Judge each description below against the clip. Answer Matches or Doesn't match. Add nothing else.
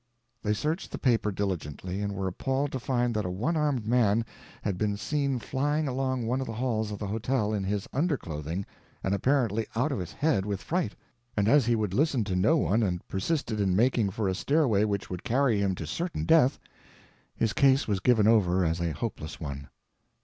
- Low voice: Matches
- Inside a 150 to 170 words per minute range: Doesn't match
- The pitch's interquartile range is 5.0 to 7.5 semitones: Matches